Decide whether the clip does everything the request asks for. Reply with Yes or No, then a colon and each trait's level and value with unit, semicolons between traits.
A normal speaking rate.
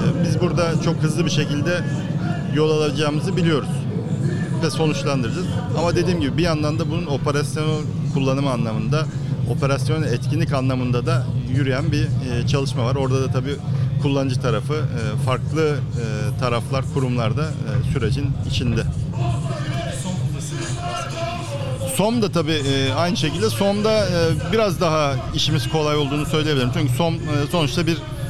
Yes: average, 120 wpm